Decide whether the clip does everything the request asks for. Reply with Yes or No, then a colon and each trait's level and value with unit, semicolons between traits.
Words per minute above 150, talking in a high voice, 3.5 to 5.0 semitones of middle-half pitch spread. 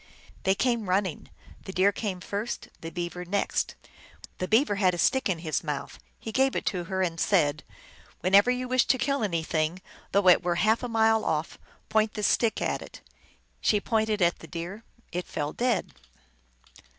Yes: average, 190 wpm; high, 195 Hz; average, 4.3 semitones